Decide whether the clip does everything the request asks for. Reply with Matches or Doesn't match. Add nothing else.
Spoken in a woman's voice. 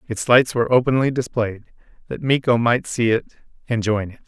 Doesn't match